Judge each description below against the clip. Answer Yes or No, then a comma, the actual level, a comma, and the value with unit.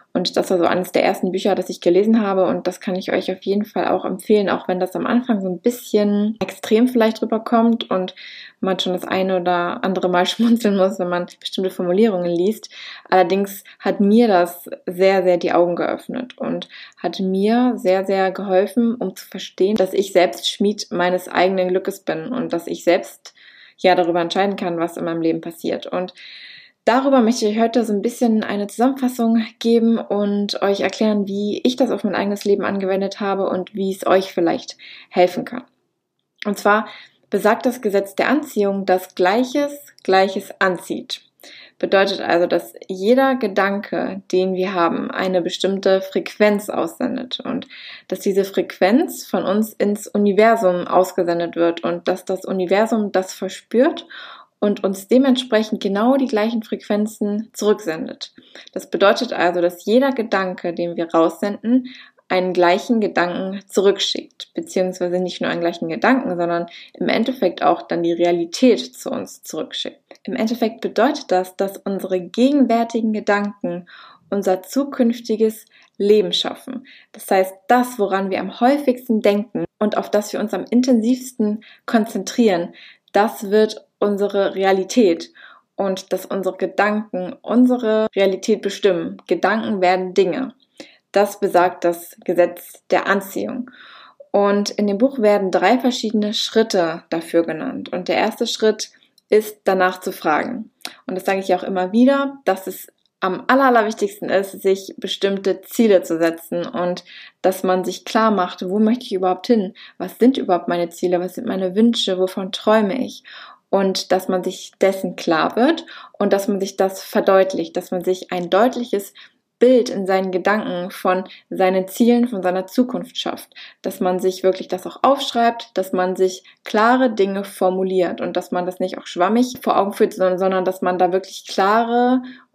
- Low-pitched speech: No, high, 195 Hz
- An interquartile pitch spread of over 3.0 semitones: Yes, average, 3.5 semitones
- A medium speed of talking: Yes, average, 165 wpm